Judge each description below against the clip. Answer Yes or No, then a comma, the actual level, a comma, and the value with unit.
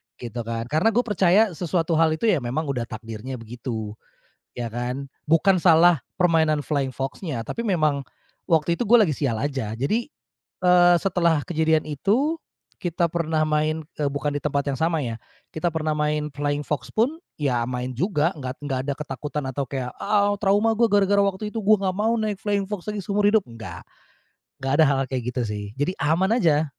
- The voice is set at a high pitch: No, medium, 155 Hz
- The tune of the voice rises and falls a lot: Yes, wide, 5.9 semitones